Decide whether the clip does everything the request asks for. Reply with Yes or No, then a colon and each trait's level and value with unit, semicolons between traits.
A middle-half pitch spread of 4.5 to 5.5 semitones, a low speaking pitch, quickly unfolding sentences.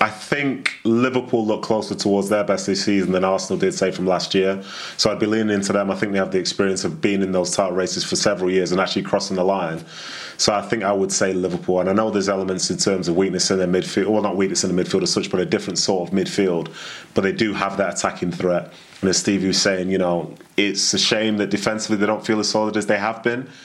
No: narrow, 2.4 semitones; low, 100 Hz; fast, 265 wpm